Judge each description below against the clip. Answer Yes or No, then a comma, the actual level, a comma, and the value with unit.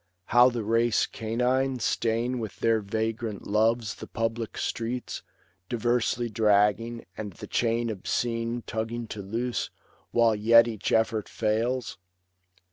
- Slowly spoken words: Yes, slow, 125 wpm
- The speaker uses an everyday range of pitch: No, narrow, 1.5 semitones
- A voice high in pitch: No, low, 115 Hz